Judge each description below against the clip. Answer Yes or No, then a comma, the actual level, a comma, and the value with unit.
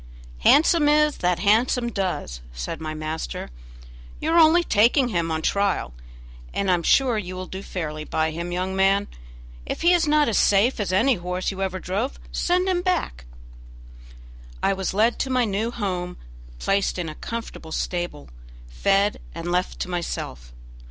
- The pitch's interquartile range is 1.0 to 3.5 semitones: No, wide, 5.6 semitones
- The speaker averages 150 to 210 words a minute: Yes, average, 170 wpm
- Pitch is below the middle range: No, high, 195 Hz